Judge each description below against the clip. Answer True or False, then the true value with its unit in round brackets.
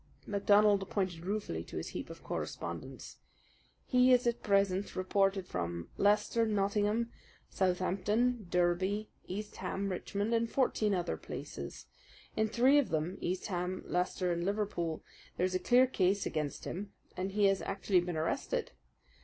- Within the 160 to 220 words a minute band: False (145 wpm)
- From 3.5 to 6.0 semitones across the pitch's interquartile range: False (2.7 semitones)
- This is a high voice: True (195 Hz)